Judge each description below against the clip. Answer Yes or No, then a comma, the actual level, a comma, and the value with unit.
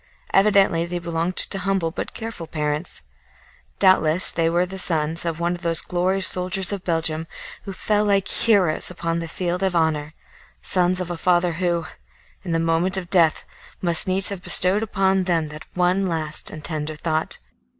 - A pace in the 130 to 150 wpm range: No, average, 170 wpm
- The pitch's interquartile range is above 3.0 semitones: No, narrow, 2.4 semitones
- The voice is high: No, medium, 175 Hz